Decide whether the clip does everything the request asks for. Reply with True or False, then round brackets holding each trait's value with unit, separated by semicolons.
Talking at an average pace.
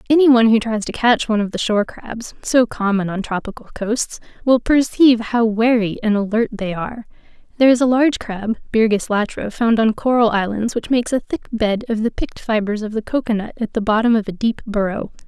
False (215 wpm)